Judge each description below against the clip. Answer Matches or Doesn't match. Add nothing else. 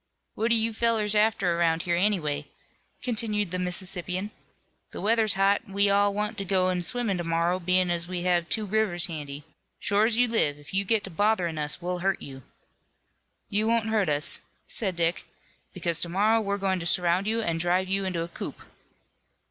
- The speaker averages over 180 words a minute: Matches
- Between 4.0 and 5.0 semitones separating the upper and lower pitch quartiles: Doesn't match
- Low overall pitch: Doesn't match